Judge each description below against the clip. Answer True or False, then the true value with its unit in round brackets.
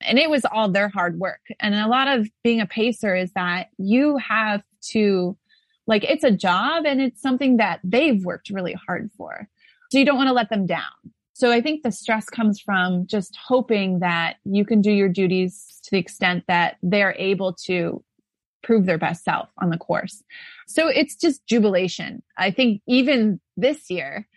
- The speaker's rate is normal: True (195 wpm)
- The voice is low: False (210 Hz)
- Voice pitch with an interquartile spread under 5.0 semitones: False (5.3 semitones)